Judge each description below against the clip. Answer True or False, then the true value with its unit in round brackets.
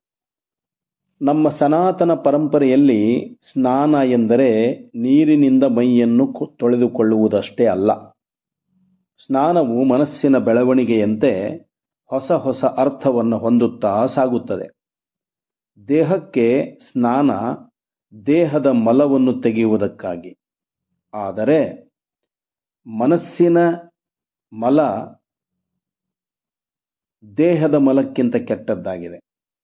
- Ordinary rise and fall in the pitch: False (6.1 semitones)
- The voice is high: False (140 Hz)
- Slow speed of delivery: True (55 wpm)